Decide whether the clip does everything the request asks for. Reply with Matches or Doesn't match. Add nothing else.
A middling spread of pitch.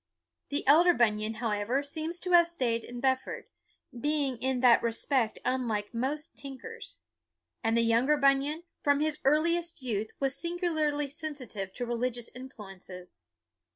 Matches